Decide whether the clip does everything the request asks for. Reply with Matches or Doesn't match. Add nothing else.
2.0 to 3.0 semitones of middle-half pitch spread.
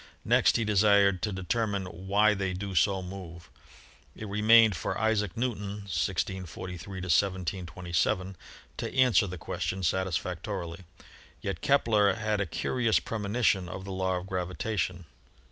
Matches